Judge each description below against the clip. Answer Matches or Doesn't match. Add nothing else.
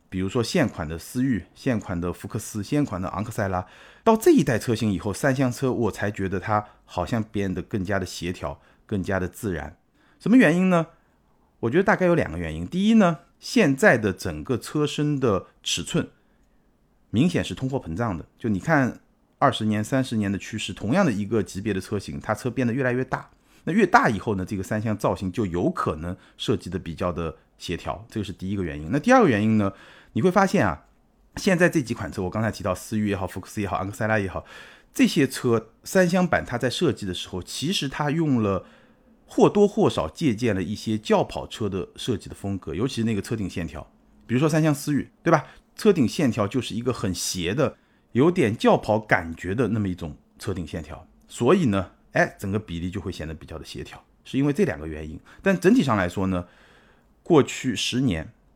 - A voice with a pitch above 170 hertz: Doesn't match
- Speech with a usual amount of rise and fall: Doesn't match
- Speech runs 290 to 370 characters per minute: Matches